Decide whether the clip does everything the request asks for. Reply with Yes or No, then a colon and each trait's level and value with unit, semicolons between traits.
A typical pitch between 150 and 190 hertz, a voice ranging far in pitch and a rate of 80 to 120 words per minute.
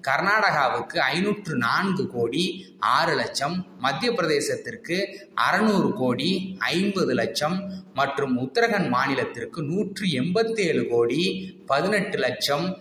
Yes: medium, 185 Hz; wide, 6.5 semitones; average, 95 wpm